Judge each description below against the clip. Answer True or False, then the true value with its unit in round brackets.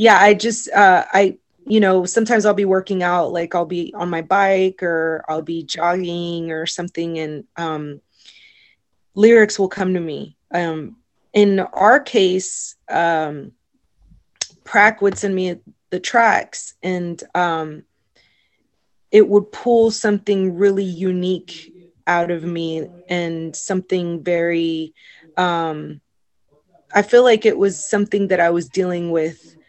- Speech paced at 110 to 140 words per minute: True (135 wpm)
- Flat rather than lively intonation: False (3.2 semitones)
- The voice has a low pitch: False (180 Hz)